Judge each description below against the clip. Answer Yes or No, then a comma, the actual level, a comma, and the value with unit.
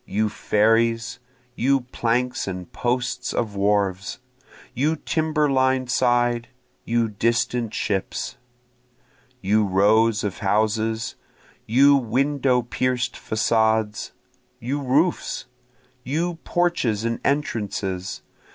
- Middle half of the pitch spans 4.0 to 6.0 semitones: No, average, 3.5 semitones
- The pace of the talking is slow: Yes, slow, 95 wpm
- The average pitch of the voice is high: No, low, 115 Hz